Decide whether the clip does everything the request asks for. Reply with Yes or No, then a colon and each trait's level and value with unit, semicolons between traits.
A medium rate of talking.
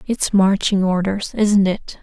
Yes: average, 150 wpm